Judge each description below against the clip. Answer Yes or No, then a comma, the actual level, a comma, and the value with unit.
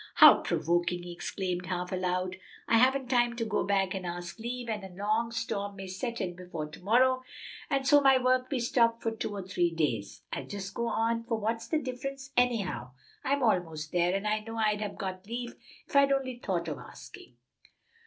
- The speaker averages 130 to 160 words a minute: No, fast, 205 wpm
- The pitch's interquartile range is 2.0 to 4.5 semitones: No, average, 4.9 semitones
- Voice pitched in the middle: No, high, 215 Hz